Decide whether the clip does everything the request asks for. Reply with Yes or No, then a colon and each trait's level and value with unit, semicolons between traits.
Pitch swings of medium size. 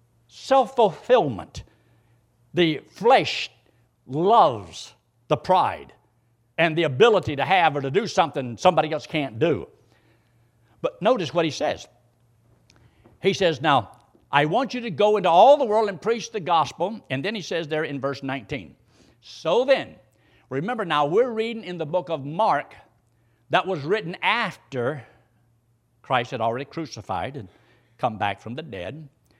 No: wide, 7.6 semitones